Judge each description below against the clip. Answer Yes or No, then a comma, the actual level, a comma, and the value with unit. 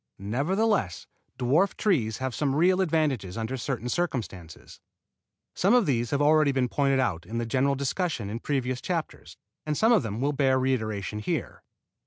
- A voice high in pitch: No, low, 130 Hz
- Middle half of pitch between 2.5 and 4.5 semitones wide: No, average, 5.1 semitones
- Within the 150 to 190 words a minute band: Yes, average, 165 wpm